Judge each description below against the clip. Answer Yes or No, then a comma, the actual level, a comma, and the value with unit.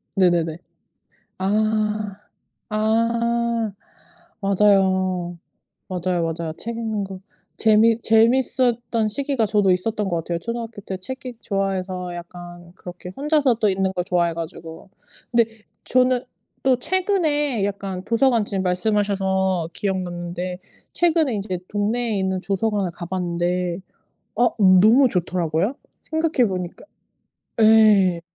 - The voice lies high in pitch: Yes, high, 200 Hz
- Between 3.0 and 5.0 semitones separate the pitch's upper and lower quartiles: Yes, average, 4.1 semitones